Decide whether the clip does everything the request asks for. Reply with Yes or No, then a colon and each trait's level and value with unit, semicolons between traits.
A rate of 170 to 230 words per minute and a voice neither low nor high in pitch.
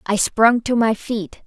No: fast, 205 wpm; high, 220 Hz